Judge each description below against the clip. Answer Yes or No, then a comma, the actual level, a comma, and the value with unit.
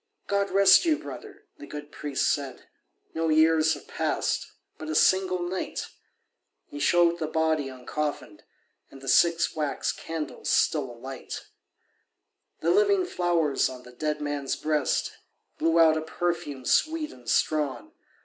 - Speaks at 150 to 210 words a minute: No, average, 140 wpm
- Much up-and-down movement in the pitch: No, average, 3.3 semitones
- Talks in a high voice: No, medium, 155 Hz